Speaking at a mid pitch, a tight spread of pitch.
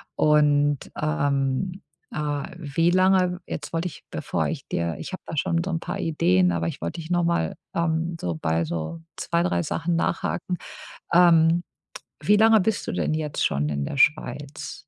No: medium, 160 Hz; average, 4.7 semitones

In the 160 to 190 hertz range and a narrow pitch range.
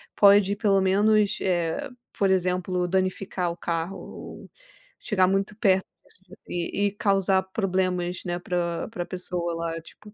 Yes: medium, 185 Hz; narrow, 1.9 semitones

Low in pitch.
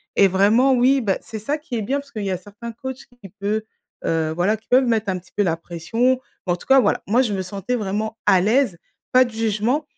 No: high, 220 Hz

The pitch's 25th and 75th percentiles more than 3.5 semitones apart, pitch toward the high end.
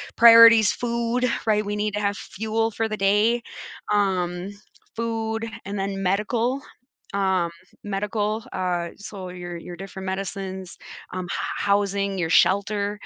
No: average, 2.7 semitones; high, 200 Hz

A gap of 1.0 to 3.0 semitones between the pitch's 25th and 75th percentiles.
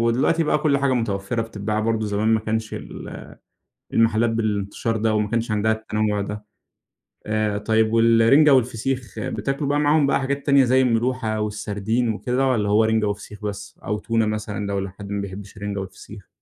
Yes: narrow, 2.6 semitones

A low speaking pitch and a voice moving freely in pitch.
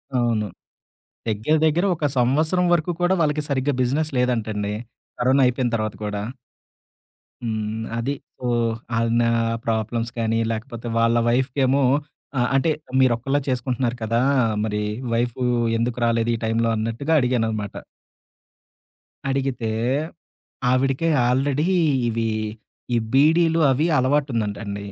No: low, 120 Hz; average, 3.2 semitones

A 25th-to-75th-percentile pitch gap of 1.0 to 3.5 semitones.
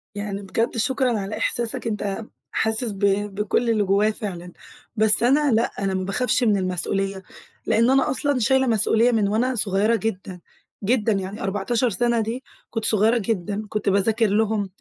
Yes: average, 2.9 semitones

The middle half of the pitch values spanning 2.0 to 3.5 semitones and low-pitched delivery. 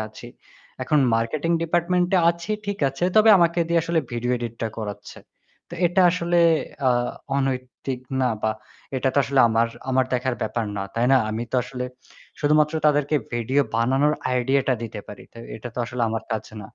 No: average, 5.0 semitones; low, 130 Hz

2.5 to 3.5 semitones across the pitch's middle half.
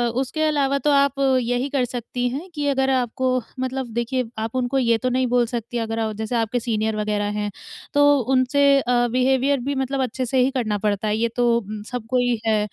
Yes: average, 2.8 semitones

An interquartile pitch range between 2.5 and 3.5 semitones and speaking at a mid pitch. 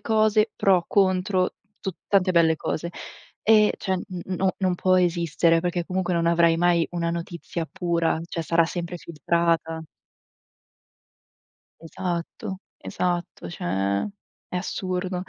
No: narrow, 1.9 semitones; medium, 175 Hz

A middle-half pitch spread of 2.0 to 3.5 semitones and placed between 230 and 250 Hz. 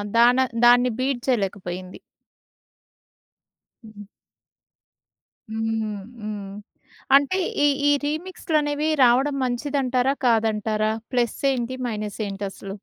No: average, 4.1 semitones; high, 240 Hz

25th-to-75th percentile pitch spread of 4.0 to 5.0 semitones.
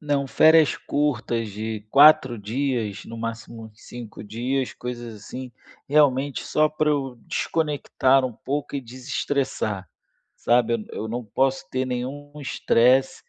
No: average, 3.5 semitones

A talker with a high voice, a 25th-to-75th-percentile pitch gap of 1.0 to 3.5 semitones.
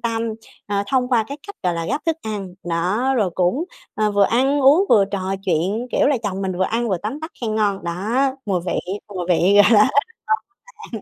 No: high, 210 Hz; average, 4.9 semitones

